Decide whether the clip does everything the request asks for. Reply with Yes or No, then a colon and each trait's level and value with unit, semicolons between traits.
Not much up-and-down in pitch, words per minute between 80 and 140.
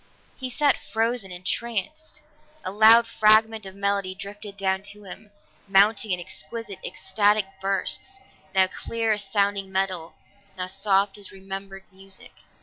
Yes: narrow, 2.2 semitones; slow, 135 wpm